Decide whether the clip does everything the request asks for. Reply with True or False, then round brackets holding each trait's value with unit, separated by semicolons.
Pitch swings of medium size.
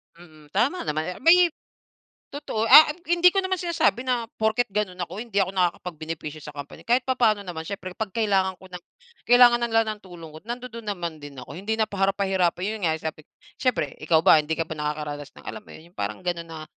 False (6.4 semitones)